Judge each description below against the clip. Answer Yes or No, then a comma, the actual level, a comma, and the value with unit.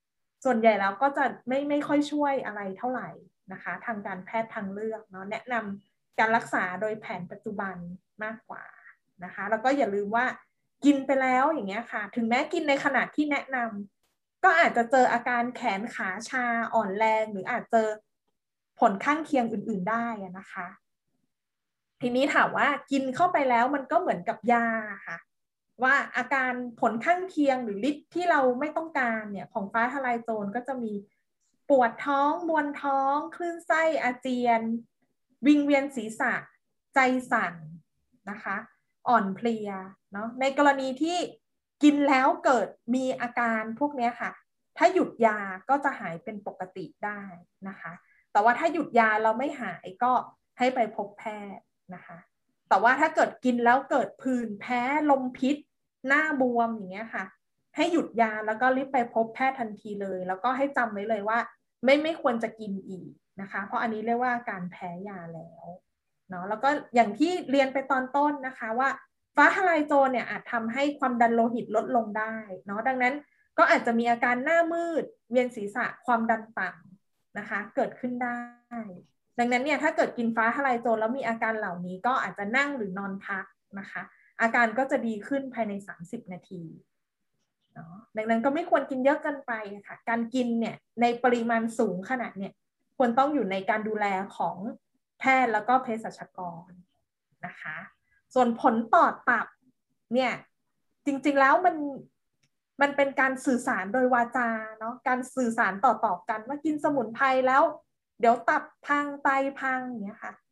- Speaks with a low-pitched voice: No, high, 235 Hz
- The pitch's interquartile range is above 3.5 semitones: Yes, average, 3.9 semitones